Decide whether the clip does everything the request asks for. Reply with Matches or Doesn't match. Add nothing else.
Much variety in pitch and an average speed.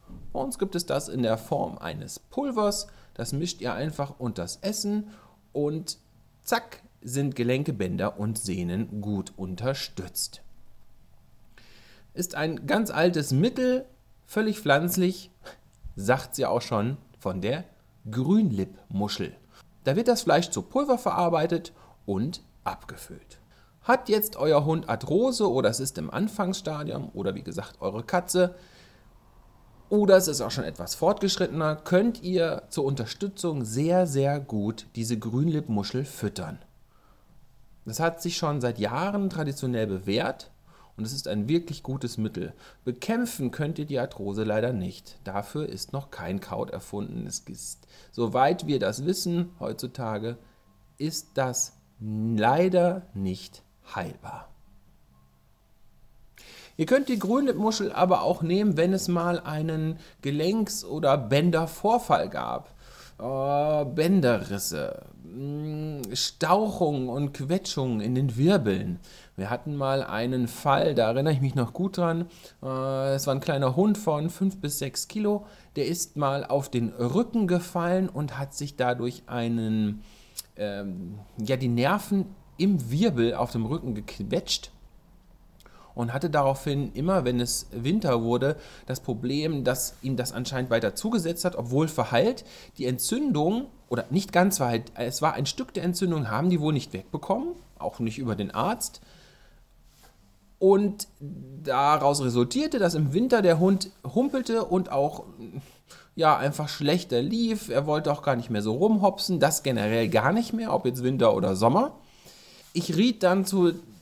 Matches